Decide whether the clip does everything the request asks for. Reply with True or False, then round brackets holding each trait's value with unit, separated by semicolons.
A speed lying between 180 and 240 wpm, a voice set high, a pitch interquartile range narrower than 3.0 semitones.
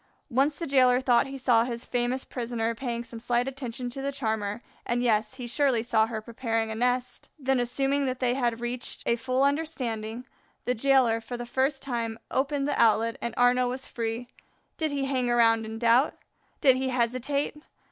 True (190 wpm; 245 Hz; 2.4 semitones)